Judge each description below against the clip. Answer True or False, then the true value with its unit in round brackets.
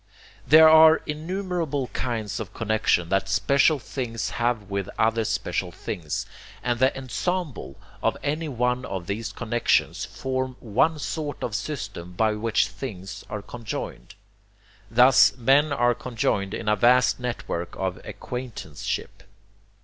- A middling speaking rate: False (130 wpm)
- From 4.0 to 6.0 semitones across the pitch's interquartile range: True (4.4 semitones)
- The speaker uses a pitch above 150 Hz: False (120 Hz)